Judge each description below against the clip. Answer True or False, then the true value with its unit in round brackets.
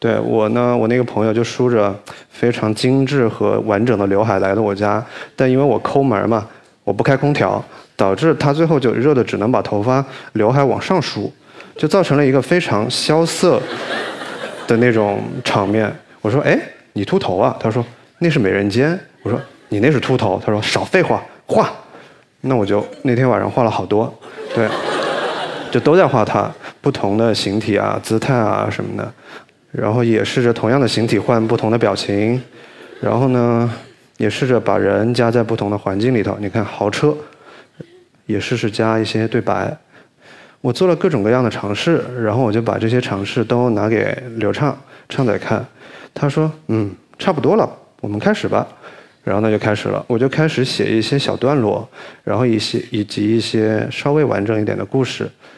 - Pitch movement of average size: True (4.0 semitones)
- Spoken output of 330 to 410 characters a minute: False (265 characters per minute)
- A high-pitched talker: False (115 Hz)